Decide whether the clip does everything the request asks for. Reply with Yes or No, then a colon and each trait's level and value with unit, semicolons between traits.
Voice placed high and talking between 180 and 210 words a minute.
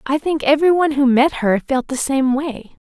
Yes: very high, 275 Hz; fast, 205 wpm